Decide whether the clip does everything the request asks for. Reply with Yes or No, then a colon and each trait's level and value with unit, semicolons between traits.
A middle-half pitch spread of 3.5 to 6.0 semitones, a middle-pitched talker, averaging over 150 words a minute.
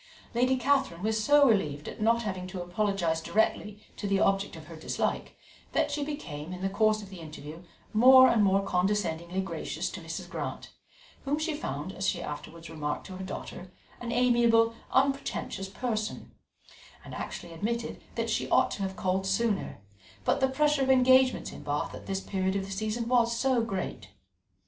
No: average, 4.7 semitones; high, 200 Hz; average, 180 wpm